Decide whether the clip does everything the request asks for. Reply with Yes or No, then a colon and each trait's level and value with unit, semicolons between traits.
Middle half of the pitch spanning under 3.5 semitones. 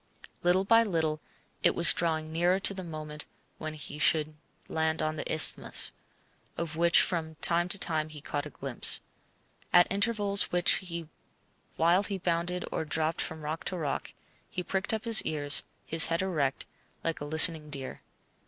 Yes: narrow, 2.6 semitones